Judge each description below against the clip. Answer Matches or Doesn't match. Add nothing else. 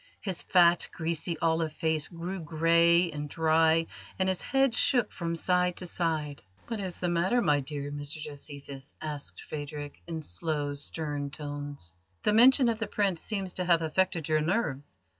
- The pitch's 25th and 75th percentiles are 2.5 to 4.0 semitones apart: Matches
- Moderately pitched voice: Matches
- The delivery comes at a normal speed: Matches